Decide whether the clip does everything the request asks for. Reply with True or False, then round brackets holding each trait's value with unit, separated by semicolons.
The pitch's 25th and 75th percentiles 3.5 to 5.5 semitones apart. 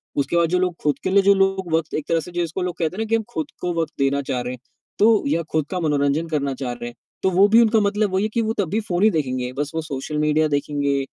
True (5.2 semitones)